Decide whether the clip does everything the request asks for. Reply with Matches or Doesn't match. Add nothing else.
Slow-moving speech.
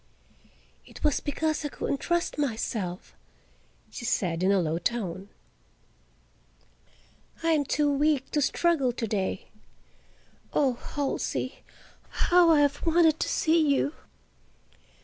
Matches